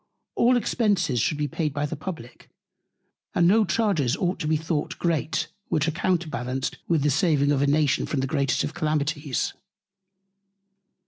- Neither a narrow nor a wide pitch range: Yes, average, 3.4 semitones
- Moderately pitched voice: Yes, medium, 155 Hz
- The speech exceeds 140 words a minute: Yes, average, 155 wpm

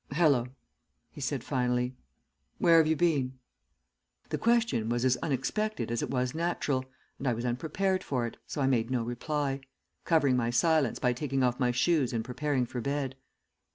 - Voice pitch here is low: Yes, low, 130 Hz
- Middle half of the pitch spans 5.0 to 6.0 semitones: No, average, 3.8 semitones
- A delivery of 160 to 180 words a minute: Yes, average, 175 wpm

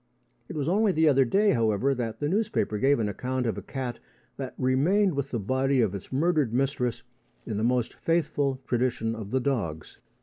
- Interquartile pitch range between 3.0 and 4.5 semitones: Yes, average, 4.1 semitones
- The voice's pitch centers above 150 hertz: No, low, 130 Hz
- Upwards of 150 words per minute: Yes, average, 195 wpm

